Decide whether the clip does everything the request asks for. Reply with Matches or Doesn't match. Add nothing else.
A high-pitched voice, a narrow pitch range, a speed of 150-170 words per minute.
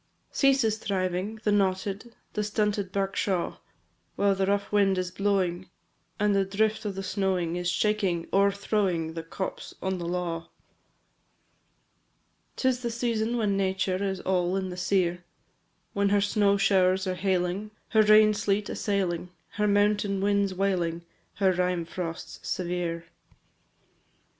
Doesn't match